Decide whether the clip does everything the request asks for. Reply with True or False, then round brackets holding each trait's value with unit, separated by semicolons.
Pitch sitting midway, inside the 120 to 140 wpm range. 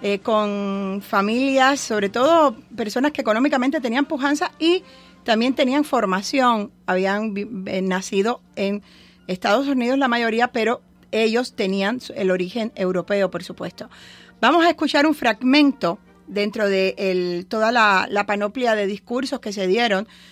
False (220 Hz; 135 wpm)